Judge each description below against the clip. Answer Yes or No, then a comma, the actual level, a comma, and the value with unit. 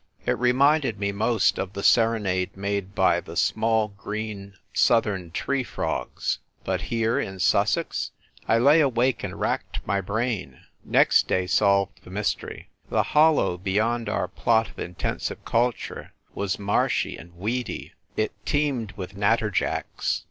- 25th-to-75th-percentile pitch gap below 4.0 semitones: Yes, average, 3.3 semitones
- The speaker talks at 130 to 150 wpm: Yes, average, 140 wpm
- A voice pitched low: Yes, low, 105 Hz